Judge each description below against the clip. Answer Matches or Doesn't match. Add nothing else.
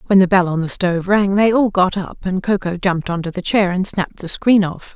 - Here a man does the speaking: Doesn't match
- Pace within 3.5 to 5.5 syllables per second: Doesn't match